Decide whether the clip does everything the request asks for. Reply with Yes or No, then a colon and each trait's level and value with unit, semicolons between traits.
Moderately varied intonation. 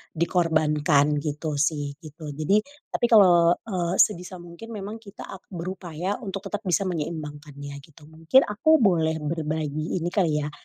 Yes: average, 3.8 semitones